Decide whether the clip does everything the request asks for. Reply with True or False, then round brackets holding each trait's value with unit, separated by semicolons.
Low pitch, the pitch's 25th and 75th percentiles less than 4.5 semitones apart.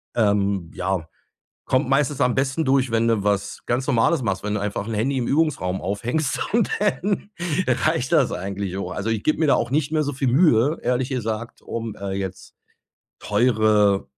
False (115 Hz; 5.2 semitones)